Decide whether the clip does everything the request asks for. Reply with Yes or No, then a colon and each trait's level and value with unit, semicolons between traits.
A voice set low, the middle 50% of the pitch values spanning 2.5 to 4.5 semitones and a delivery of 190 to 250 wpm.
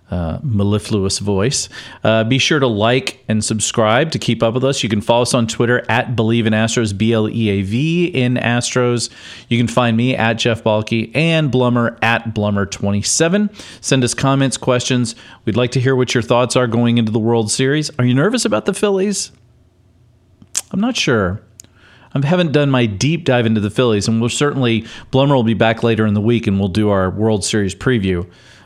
Yes: low, 120 Hz; average, 3.0 semitones; average, 195 wpm